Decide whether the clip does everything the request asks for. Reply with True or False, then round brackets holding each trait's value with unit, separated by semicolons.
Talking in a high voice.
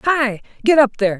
True (245 Hz)